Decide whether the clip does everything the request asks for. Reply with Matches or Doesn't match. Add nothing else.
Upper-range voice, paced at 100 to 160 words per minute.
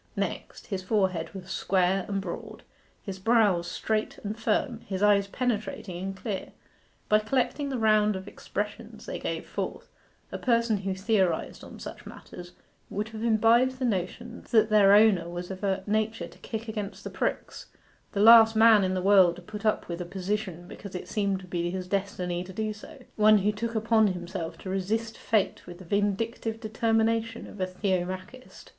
Doesn't match